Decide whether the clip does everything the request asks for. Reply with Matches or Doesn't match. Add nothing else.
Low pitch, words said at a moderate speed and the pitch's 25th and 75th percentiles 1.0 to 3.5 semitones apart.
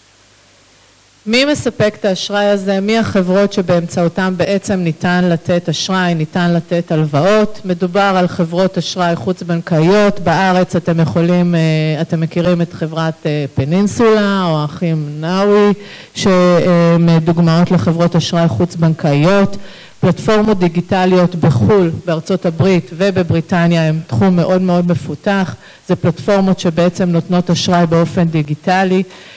Doesn't match